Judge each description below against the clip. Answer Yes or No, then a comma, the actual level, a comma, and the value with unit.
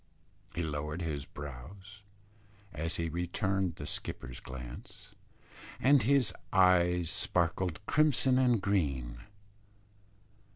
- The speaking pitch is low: Yes, very low, 85 Hz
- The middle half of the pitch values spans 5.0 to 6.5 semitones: Yes, average, 5.3 semitones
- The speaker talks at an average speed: No, slow, 95 wpm